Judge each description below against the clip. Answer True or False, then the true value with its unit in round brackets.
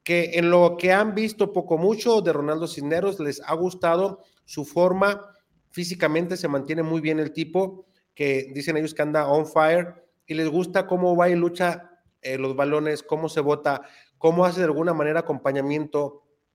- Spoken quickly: False (180 wpm)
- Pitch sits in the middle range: True (165 Hz)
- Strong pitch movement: False (3.0 semitones)